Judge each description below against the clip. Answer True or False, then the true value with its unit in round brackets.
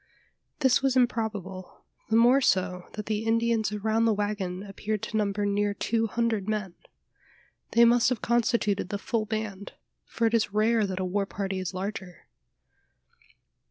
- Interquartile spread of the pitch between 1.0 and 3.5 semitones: True (2.6 semitones)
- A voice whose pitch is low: False (215 Hz)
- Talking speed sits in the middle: True (160 wpm)